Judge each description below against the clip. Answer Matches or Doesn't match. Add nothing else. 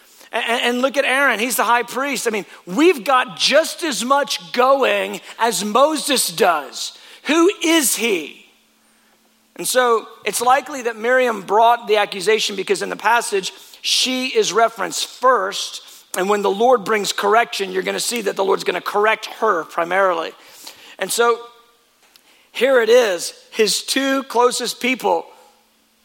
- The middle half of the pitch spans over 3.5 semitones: Matches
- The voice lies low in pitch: Doesn't match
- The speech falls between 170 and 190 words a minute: Doesn't match